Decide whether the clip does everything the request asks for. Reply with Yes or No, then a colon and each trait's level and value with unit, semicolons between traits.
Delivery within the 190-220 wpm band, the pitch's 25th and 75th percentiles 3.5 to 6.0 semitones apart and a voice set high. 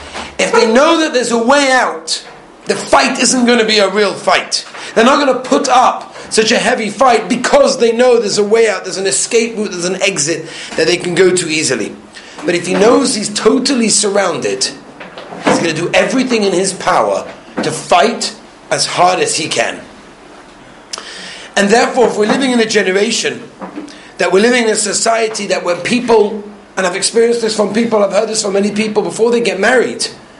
Yes: average, 200 wpm; average, 4.0 semitones; high, 220 Hz